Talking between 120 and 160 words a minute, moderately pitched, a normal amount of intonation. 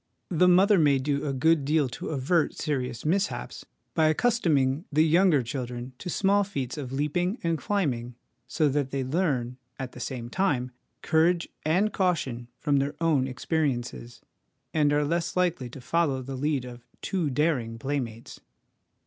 Yes: average, 155 wpm; medium, 145 Hz; average, 4.6 semitones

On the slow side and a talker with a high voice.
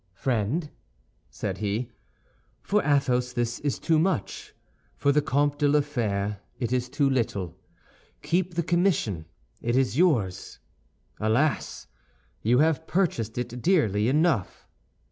No: slow, 125 wpm; low, 130 Hz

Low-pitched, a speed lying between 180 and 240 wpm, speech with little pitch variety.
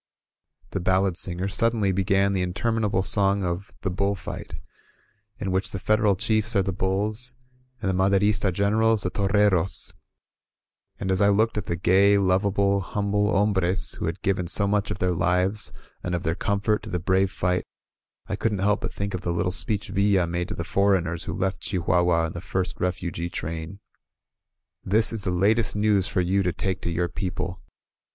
Yes: very low, 95 Hz; average, 190 wpm; narrow, 2.1 semitones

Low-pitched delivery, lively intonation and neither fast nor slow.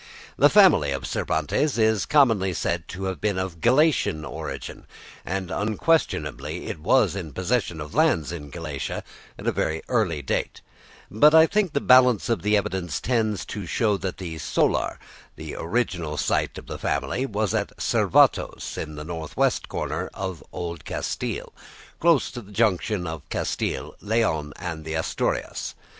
Yes: very low, 95 Hz; wide, 5.9 semitones; average, 160 wpm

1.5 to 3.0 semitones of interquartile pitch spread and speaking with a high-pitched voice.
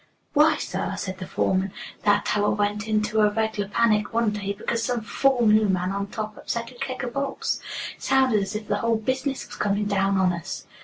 Yes: narrow, 2.5 semitones; high, 215 Hz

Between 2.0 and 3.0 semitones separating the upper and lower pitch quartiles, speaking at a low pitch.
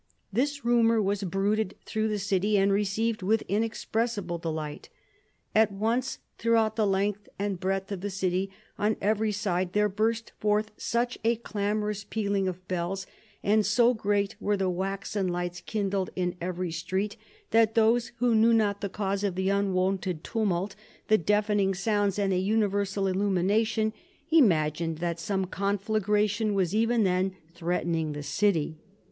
No: narrow, 2.5 semitones; high, 200 Hz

